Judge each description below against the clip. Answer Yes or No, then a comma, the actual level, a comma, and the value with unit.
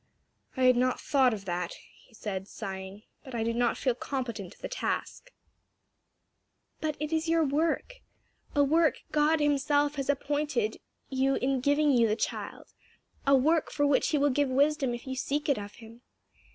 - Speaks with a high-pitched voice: Yes, very high, 270 Hz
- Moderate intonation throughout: Yes, average, 3.8 semitones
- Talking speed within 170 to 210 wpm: Yes, average, 180 wpm